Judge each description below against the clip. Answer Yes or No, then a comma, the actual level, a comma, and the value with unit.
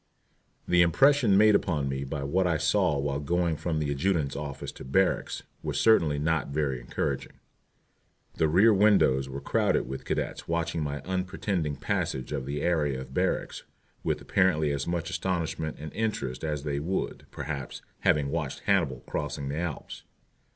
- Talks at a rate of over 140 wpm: Yes, average, 160 wpm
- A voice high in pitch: No, very low, 75 Hz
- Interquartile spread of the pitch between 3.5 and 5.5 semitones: Yes, average, 4.0 semitones